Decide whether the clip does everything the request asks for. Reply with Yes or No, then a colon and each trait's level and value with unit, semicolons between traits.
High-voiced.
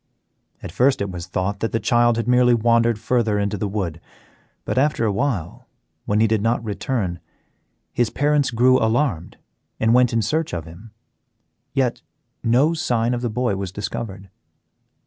No: low, 115 Hz